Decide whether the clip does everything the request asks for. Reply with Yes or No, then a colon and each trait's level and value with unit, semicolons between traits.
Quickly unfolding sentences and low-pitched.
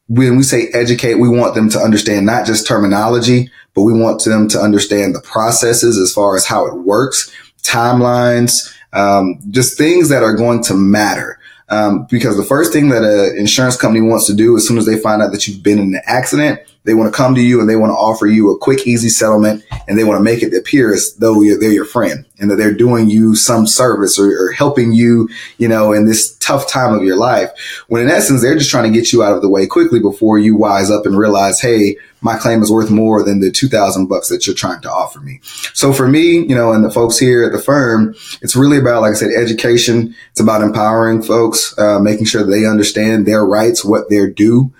Yes: fast, 240 wpm; low, 110 Hz